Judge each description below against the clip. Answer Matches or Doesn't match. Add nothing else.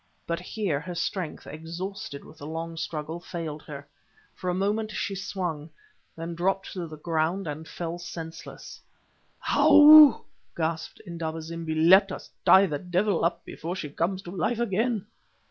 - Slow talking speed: Doesn't match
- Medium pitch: Matches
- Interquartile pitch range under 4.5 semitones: Matches